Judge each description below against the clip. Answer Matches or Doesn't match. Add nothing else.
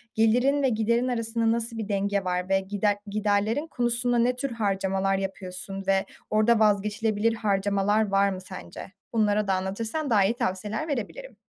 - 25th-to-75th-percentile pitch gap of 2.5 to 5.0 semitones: Matches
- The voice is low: Doesn't match